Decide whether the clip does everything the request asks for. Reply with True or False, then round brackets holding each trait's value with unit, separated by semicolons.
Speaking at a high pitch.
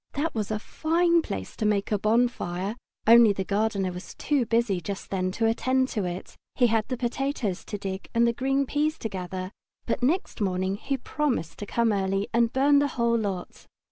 True (225 Hz)